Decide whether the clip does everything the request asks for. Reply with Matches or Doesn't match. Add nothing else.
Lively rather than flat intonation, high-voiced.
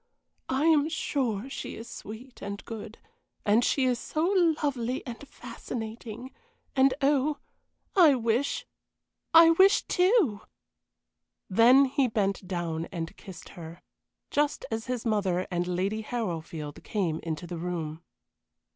Matches